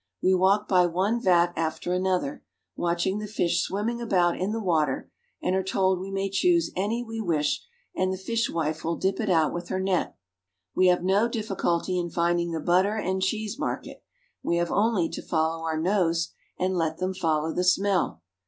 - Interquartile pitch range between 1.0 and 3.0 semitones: Yes, narrow, 2.5 semitones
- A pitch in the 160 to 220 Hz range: Yes, medium, 185 Hz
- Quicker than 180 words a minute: Yes, average, 190 wpm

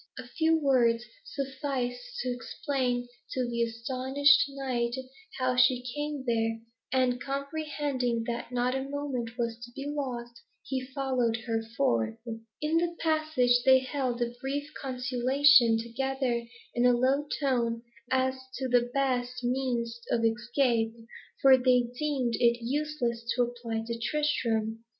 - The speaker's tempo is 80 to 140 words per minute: Yes, slow, 135 wpm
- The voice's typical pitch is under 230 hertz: No, very high, 250 Hz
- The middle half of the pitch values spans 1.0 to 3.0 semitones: Yes, narrow, 2.6 semitones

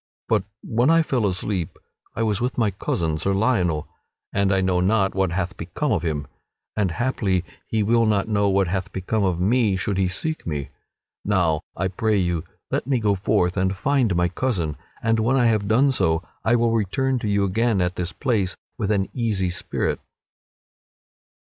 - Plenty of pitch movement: No, average, 3.8 semitones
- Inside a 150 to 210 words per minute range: Yes, average, 185 wpm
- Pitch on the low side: Yes, low, 100 Hz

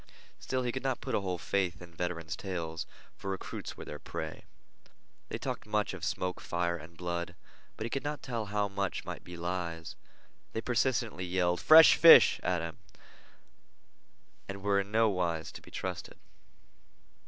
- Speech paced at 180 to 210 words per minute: No, average, 170 wpm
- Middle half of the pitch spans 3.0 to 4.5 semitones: Yes, average, 4.0 semitones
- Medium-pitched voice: No, very low, 90 Hz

